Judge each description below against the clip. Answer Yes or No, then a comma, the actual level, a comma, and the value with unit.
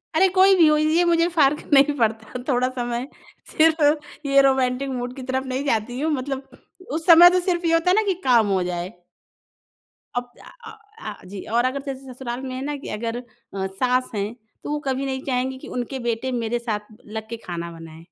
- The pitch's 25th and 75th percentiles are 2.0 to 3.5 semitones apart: No, average, 3.9 semitones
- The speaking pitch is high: Yes, very high, 260 Hz